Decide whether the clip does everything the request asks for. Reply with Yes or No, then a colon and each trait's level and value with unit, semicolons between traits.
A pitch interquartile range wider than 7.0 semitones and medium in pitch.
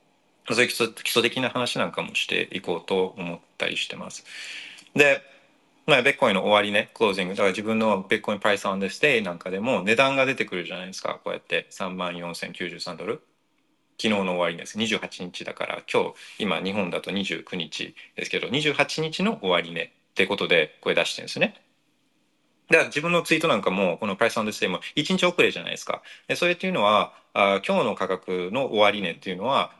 No: wide, 8.2 semitones; low, 110 Hz